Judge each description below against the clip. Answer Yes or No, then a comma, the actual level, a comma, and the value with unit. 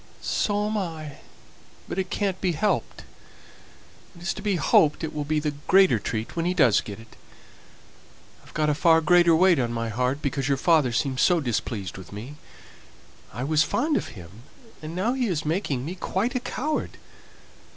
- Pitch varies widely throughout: Yes, wide, 6.4 semitones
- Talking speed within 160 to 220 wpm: Yes, average, 180 wpm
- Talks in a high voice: No, medium, 155 Hz